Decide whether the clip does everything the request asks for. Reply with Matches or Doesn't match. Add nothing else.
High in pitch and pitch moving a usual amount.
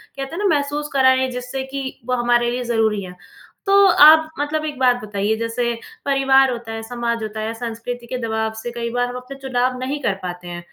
Matches